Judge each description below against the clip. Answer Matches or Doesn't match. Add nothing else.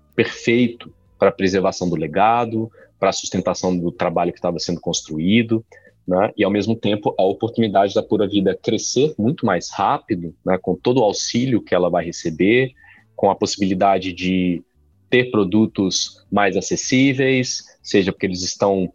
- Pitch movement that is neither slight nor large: Matches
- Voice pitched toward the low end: Matches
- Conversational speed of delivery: Matches